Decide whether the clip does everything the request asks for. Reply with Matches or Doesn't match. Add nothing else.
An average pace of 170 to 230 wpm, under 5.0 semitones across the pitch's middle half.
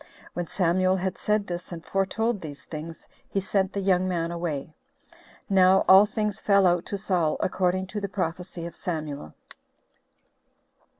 Doesn't match